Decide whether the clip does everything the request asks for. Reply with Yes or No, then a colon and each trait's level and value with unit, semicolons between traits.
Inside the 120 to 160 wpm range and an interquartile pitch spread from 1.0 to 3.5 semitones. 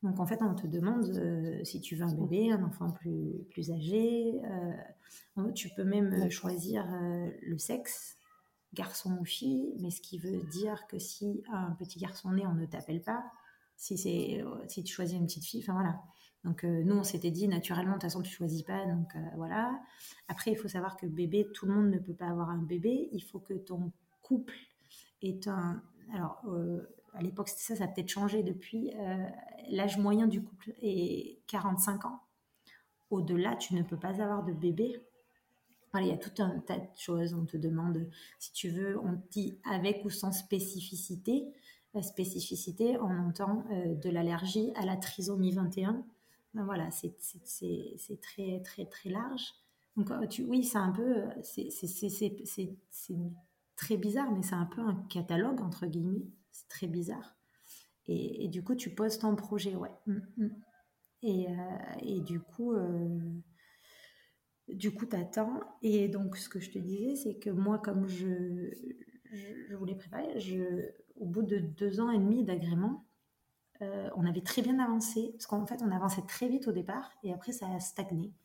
No: average, 190 wpm; average, 3.2 semitones